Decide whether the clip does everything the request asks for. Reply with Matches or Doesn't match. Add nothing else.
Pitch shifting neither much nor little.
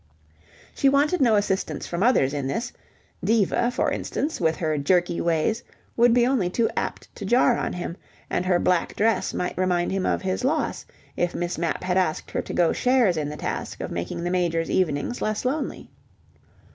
Doesn't match